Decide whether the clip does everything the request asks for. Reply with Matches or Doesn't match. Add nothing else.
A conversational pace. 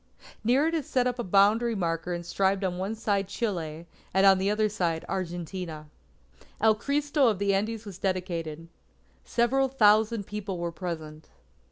Matches